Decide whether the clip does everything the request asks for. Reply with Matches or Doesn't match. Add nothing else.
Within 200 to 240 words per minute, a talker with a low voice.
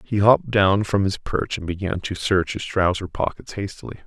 Matches